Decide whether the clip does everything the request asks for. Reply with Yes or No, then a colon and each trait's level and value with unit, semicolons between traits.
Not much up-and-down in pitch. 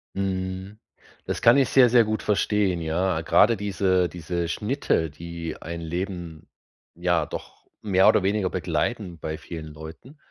No: average, 3.6 semitones